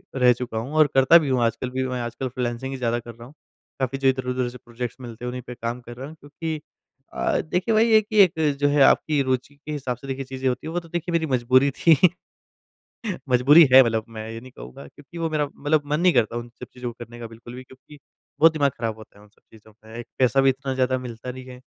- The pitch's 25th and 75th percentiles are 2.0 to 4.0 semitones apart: Yes, average, 3.3 semitones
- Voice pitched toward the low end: Yes, low, 130 Hz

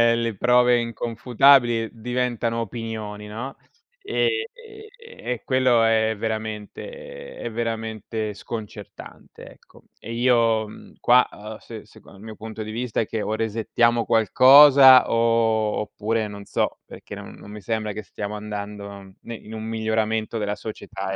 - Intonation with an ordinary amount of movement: No, narrow, 1.9 semitones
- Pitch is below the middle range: Yes, low, 115 Hz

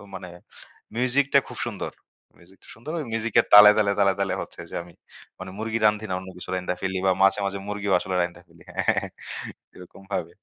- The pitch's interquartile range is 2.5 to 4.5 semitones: Yes, average, 2.9 semitones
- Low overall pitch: Yes, low, 100 Hz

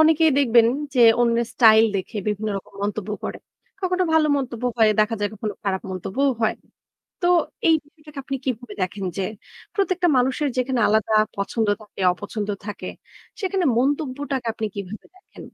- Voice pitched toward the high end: Yes, high, 235 Hz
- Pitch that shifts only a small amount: No, wide, 5.4 semitones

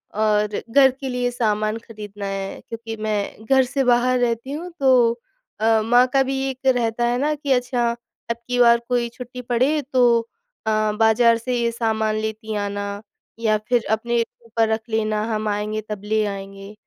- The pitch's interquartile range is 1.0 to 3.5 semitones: Yes, narrow, 2.6 semitones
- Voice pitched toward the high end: Yes, high, 230 Hz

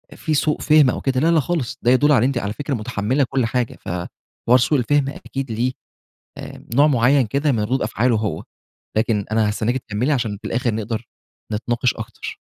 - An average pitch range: Yes, average, 3.7 semitones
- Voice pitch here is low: Yes, low, 125 Hz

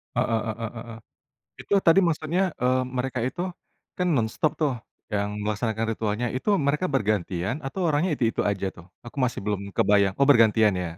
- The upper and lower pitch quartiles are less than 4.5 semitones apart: No, average, 5.2 semitones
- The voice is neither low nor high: No, low, 115 Hz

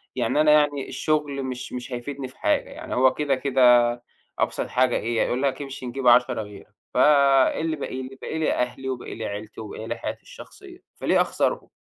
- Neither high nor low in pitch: No, low, 130 Hz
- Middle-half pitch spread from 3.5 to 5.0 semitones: No, narrow, 2.6 semitones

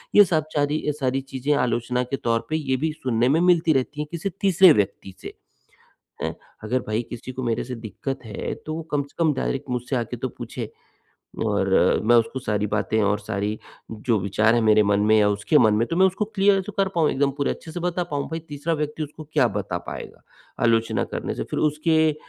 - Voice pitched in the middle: No, low, 130 Hz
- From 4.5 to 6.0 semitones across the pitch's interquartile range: Yes, wide, 5.5 semitones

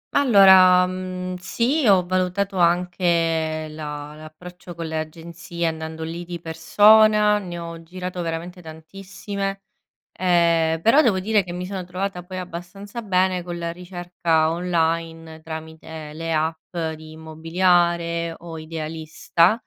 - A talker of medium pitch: Yes, medium, 175 Hz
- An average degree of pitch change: No, narrow, 2.3 semitones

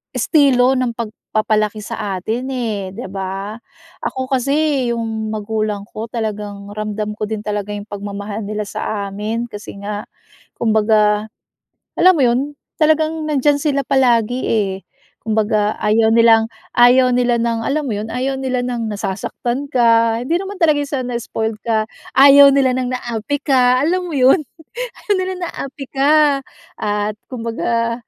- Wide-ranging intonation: No, average, 3.9 semitones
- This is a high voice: Yes, high, 230 Hz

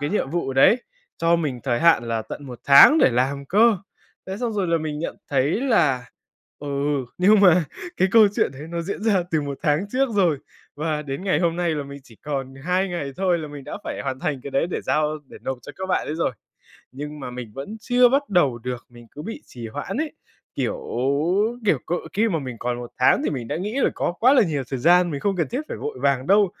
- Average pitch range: No, wide, 6.0 semitones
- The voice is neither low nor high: Yes, medium, 155 Hz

